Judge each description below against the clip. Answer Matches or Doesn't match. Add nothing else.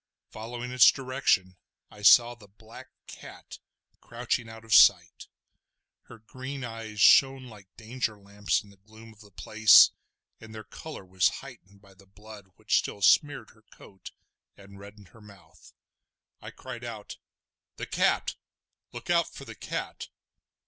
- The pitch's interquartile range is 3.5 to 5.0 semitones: Doesn't match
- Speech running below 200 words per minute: Matches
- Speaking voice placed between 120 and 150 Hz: Doesn't match